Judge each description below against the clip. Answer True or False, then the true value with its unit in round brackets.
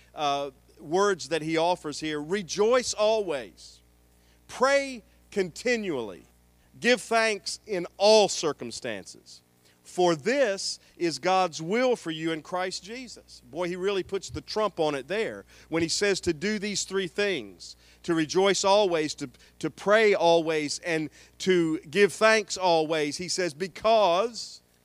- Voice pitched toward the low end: False (175 Hz)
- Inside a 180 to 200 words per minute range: False (140 wpm)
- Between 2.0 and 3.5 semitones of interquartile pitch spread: False (5.3 semitones)